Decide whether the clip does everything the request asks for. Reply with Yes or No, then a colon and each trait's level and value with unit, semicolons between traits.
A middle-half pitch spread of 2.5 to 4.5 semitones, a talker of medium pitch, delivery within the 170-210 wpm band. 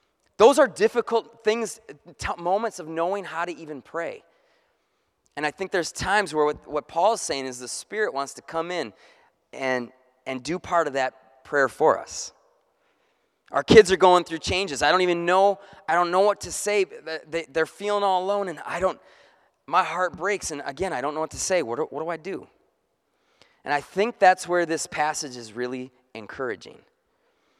No: average, 5.3 semitones; medium, 175 Hz; average, 195 wpm